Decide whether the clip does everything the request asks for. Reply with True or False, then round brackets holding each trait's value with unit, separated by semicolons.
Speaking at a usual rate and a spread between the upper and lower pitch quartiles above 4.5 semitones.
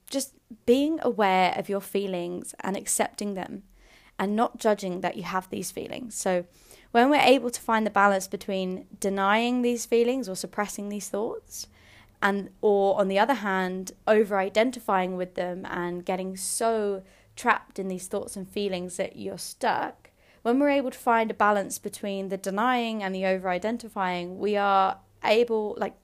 False (165 wpm; 3.4 semitones)